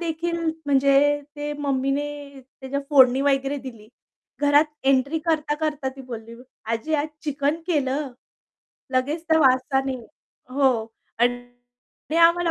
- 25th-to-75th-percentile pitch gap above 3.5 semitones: No, narrow, 2.5 semitones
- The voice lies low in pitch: No, very high, 280 Hz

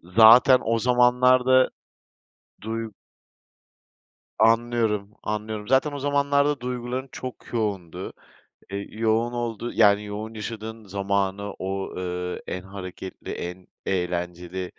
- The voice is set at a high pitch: No, low, 110 Hz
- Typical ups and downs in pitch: Yes, average, 4.0 semitones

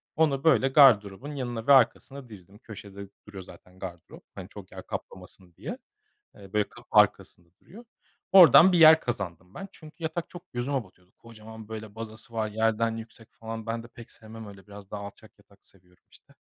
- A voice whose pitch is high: No, low, 110 Hz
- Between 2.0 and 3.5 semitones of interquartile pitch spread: No, average, 4.8 semitones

